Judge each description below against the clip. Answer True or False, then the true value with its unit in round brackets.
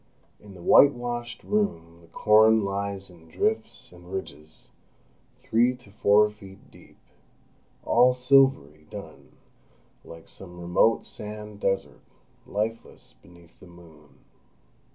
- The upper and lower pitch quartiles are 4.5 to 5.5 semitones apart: True (4.8 semitones)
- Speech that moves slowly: True (110 wpm)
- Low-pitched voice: True (100 Hz)